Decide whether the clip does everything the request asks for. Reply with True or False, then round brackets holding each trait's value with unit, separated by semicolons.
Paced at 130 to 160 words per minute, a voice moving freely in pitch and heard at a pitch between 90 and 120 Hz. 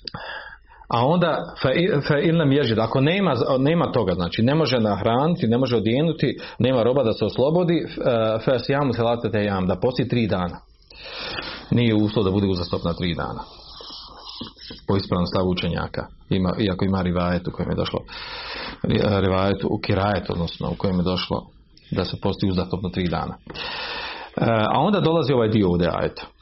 True (150 wpm; 6.7 semitones; 105 Hz)